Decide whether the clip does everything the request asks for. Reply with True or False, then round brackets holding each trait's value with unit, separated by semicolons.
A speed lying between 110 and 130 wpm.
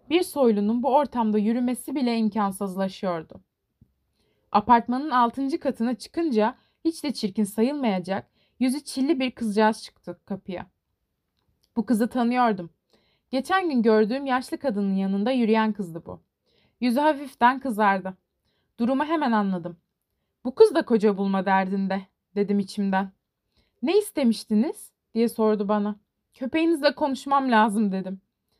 True (115 wpm)